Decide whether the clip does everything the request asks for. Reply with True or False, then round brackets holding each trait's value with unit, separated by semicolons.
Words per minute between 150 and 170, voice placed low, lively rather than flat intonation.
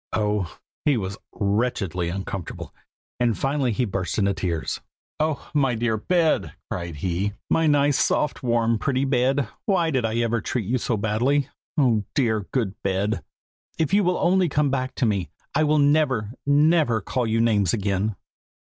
True (165 wpm; 115 Hz; 5.7 semitones)